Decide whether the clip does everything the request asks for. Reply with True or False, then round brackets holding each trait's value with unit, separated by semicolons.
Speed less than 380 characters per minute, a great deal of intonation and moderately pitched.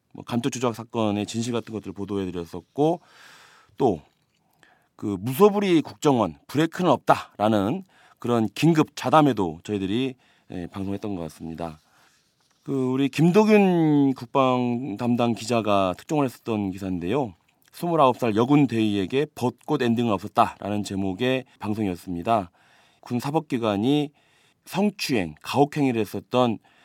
False (290 characters per minute; 5.7 semitones; 120 Hz)